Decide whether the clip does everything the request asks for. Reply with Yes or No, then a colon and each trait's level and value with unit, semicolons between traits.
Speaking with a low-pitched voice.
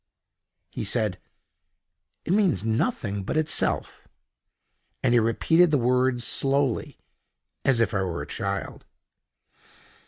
Yes: low, 125 Hz